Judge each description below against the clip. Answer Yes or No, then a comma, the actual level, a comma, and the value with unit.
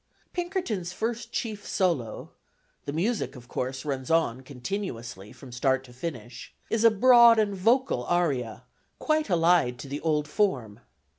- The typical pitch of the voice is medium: Yes, medium, 160 Hz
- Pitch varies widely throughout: Yes, wide, 9.0 semitones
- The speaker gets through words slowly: No, average, 145 wpm